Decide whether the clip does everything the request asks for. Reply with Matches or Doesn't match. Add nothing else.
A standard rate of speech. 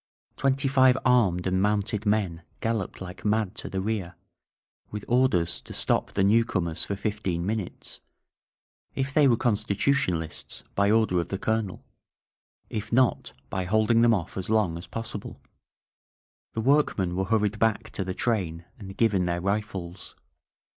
Matches